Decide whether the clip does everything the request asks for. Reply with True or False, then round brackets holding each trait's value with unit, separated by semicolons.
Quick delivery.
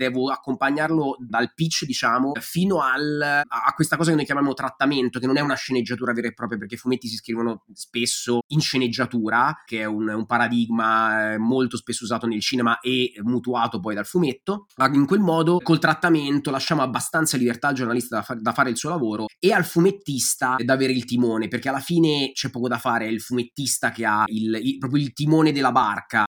True (200 wpm)